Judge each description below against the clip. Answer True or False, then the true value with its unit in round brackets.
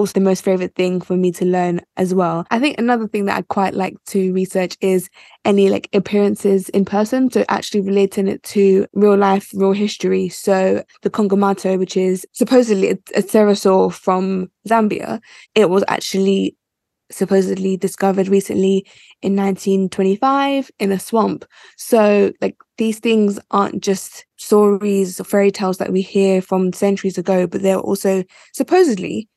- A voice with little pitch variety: True (1.5 semitones)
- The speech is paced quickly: False (160 wpm)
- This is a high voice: True (195 Hz)